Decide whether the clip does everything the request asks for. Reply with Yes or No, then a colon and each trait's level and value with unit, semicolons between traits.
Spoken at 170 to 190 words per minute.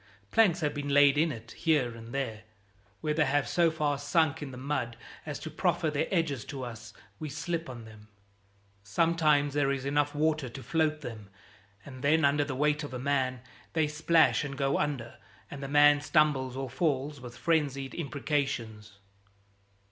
Yes: average, 180 wpm